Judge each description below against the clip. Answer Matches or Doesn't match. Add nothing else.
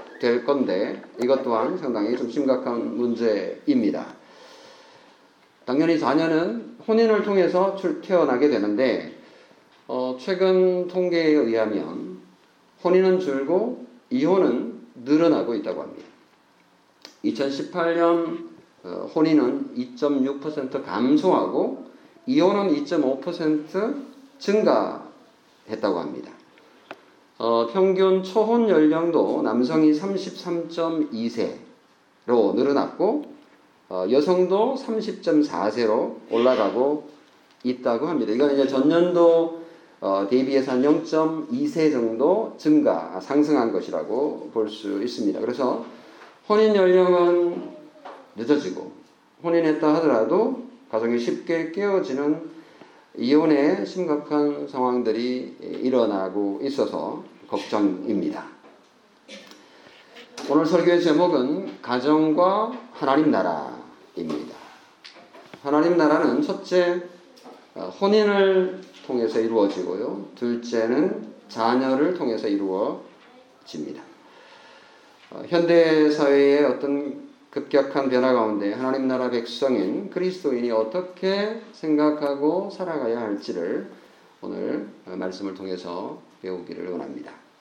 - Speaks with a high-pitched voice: Doesn't match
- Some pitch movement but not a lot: Doesn't match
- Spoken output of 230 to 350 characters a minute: Doesn't match